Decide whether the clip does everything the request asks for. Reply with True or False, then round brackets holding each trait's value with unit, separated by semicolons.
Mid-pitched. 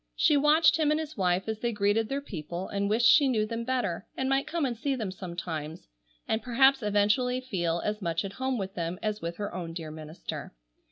False (215 Hz)